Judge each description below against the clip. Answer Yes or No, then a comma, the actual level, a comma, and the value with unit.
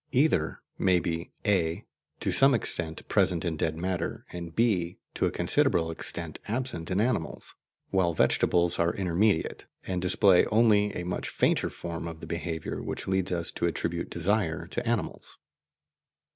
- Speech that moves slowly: No, average, 155 wpm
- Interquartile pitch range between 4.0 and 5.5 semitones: No, average, 3.3 semitones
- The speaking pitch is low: Yes, very low, 90 Hz